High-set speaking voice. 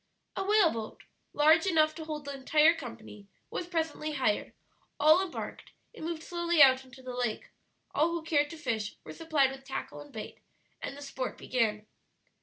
Yes: very high, 295 Hz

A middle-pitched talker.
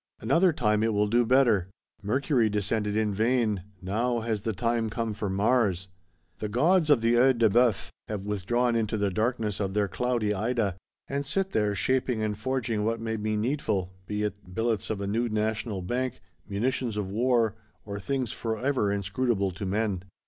No: low, 110 Hz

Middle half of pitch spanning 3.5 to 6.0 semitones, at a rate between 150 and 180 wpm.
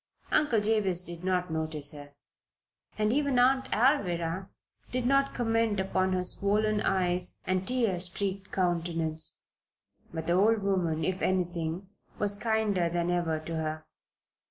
No: average, 3.9 semitones; slow, 135 wpm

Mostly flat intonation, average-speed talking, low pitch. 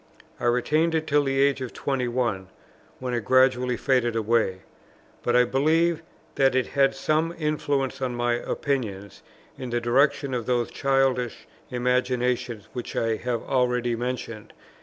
Yes: narrow, 2.2 semitones; average, 155 wpm; low, 125 Hz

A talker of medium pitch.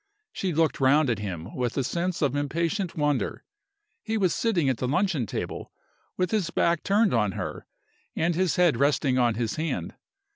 Yes: medium, 155 Hz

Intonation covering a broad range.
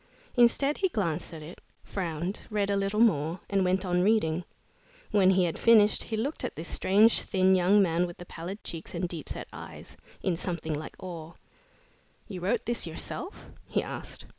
No: average, 3.7 semitones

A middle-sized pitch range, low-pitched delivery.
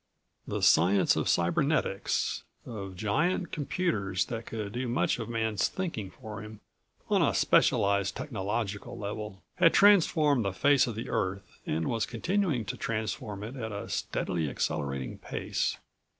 Yes: average, 4.8 semitones; low, 110 Hz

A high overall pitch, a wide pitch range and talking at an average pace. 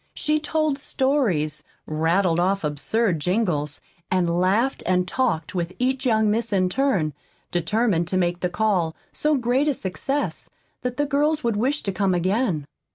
Yes: high, 200 Hz; wide, 6.9 semitones; average, 160 wpm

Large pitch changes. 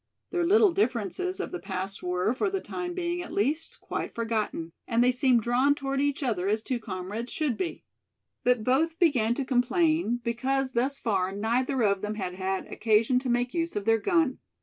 Yes: wide, 5.8 semitones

